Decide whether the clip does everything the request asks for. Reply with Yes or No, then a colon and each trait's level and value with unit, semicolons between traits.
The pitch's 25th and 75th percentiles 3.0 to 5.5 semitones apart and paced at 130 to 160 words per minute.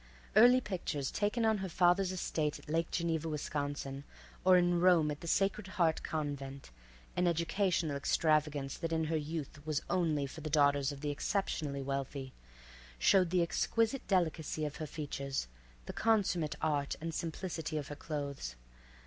Yes: average, 3.7 semitones; average, 150 wpm